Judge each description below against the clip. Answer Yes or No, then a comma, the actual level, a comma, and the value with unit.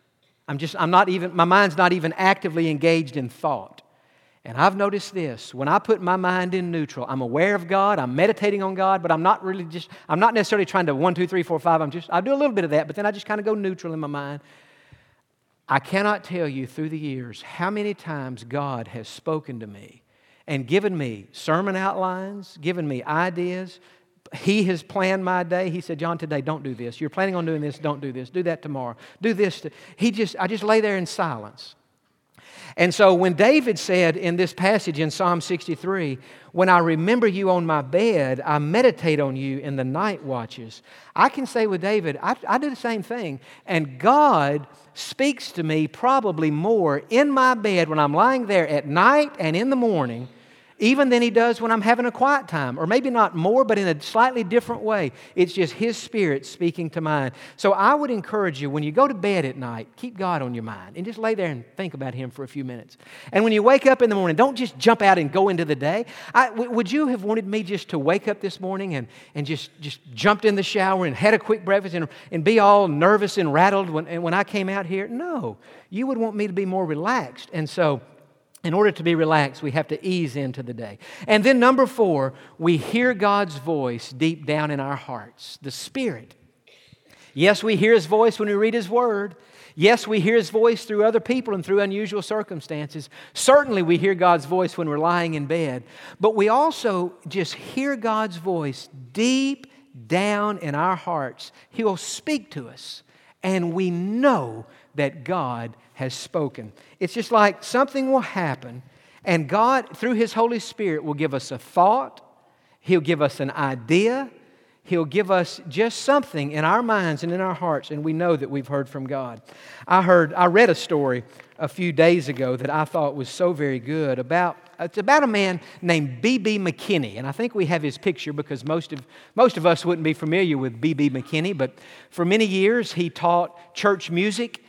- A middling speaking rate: No, fast, 215 wpm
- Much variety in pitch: Yes, wide, 5.8 semitones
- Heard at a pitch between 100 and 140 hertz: No, medium, 180 Hz